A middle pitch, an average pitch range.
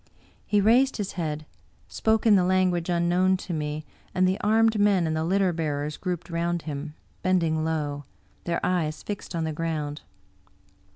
Yes: medium, 170 Hz; average, 3.1 semitones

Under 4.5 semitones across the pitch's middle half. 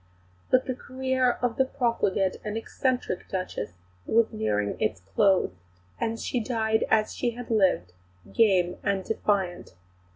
No: average, 4.9 semitones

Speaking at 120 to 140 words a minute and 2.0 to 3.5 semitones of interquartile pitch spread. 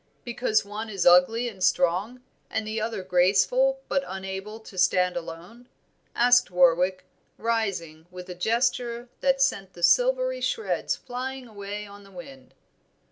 No: slow, 135 wpm; average, 5.1 semitones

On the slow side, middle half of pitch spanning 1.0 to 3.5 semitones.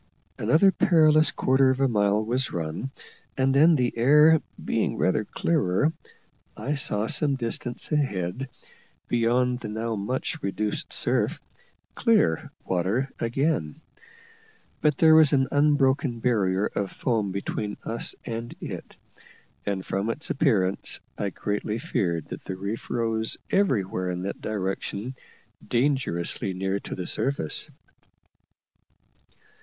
No: slow, 125 wpm; wide, 5.6 semitones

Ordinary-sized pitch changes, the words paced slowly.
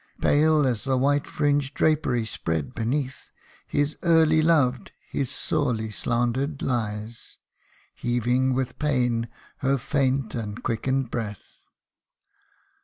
Yes: average, 3.6 semitones; slow, 110 wpm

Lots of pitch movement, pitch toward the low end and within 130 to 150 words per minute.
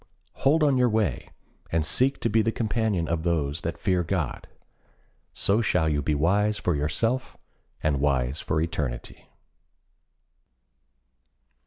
Yes: wide, 6.4 semitones; very low, 85 Hz; slow, 135 wpm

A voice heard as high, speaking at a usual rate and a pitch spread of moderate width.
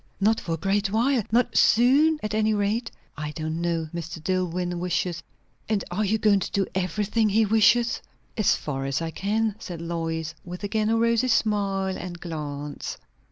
Yes: high, 195 Hz; average, 180 wpm; average, 4.4 semitones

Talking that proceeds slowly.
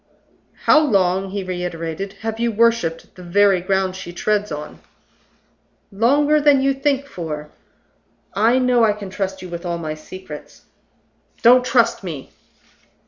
No: average, 145 wpm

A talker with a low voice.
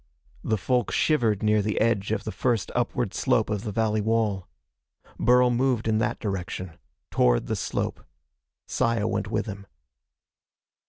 Yes: low, 110 Hz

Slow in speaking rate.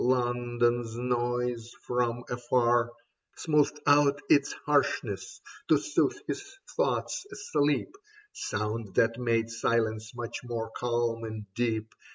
Yes: slow, 110 wpm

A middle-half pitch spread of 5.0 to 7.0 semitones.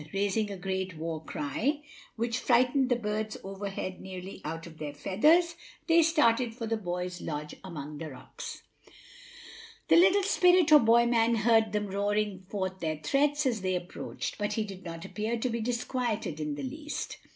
Yes: average, 5.3 semitones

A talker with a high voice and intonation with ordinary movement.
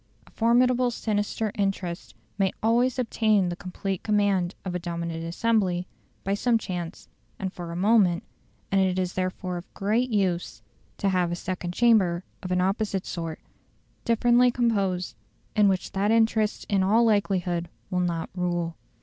Yes: high, 195 Hz; average, 3.6 semitones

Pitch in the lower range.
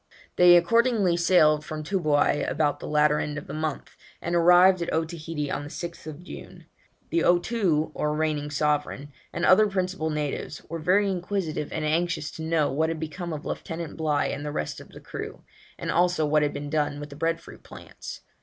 No: medium, 160 Hz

